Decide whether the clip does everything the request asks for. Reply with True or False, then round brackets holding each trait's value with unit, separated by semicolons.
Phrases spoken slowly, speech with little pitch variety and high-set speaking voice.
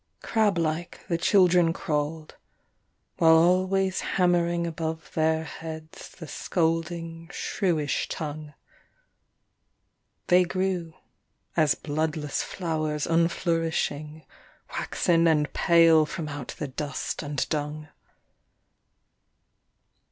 False (90 wpm; 1.9 semitones; 165 Hz)